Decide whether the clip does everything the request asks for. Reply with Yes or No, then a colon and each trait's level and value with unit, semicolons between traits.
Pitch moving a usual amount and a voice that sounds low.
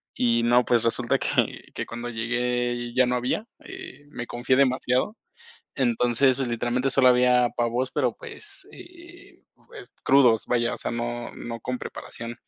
No: narrow, 1.9 semitones; low, 125 Hz